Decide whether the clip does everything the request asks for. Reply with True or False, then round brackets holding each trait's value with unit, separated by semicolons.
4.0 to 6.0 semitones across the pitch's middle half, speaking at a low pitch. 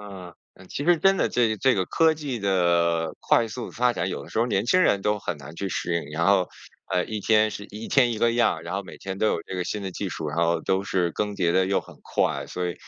True (4.3 semitones; 100 Hz)